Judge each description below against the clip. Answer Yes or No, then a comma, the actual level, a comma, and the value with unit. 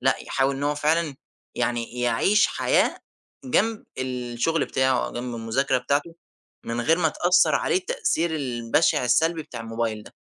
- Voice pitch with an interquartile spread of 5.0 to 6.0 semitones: Yes, average, 5.3 semitones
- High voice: No, low, 135 Hz